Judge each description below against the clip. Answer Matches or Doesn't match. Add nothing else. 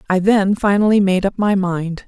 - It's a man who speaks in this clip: Doesn't match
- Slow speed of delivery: Doesn't match